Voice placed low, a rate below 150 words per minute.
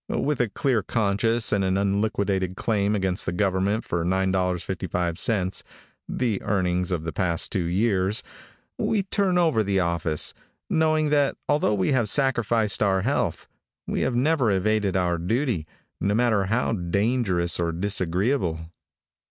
Yes: low, 100 Hz; average, 140 wpm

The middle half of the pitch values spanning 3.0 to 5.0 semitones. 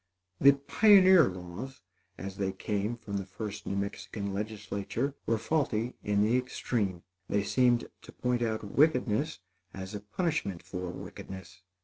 Yes: average, 4.4 semitones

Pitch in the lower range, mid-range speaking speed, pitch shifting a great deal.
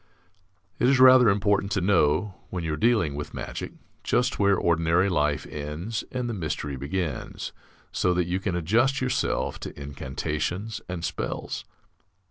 Yes: very low, 90 Hz; average, 150 wpm; wide, 6.0 semitones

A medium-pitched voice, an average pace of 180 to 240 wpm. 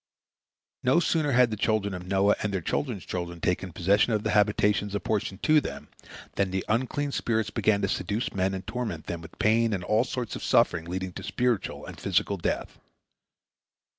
No: low, 100 Hz; average, 185 wpm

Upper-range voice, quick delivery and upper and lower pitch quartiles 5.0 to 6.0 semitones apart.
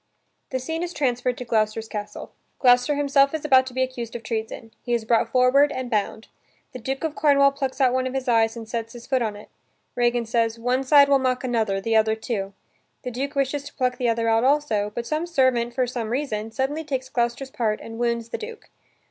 No: very high, 250 Hz; fast, 225 wpm; average, 3.0 semitones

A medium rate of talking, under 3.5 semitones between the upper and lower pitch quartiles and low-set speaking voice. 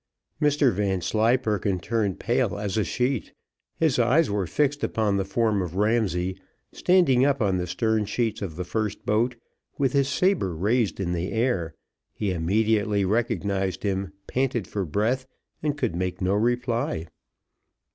No: average, 150 wpm; average, 4.4 semitones; low, 105 Hz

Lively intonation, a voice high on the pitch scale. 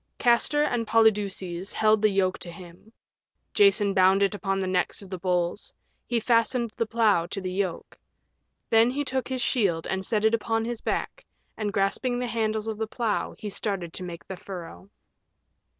No: average, 3.4 semitones; high, 210 Hz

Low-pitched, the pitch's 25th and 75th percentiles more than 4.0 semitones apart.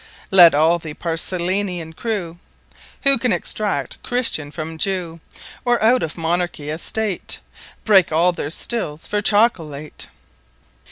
No: medium, 175 Hz; average, 4.5 semitones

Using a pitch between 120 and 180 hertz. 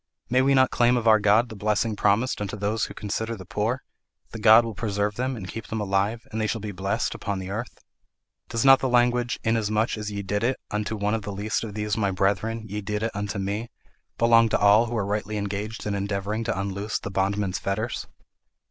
No: low, 105 Hz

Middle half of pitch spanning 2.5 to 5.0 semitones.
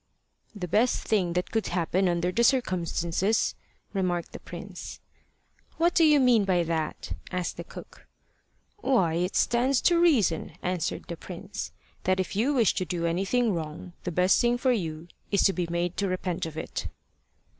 No: wide, 5.4 semitones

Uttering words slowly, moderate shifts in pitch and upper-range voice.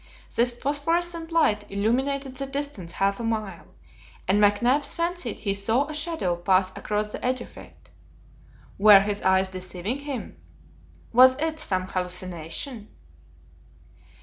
No: slow, 130 wpm; wide, 6.5 semitones; high, 225 Hz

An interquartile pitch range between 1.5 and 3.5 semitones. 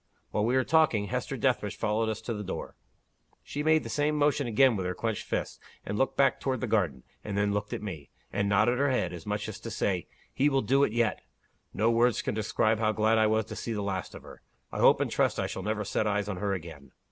Yes: average, 3.0 semitones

